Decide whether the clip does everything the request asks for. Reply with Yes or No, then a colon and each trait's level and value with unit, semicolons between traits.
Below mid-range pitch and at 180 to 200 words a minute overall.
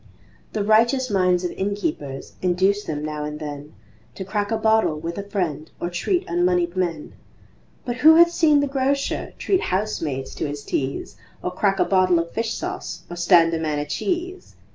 No: medium, 185 Hz; average, 185 wpm